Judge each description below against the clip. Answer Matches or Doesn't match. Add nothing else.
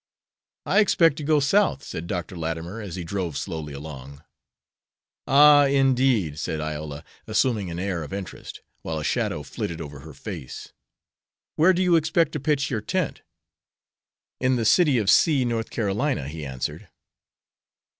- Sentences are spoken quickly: Doesn't match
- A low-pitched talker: Matches